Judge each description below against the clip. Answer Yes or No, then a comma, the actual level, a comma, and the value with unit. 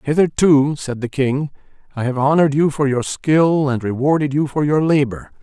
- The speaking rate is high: No, average, 190 wpm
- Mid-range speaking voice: Yes, medium, 145 Hz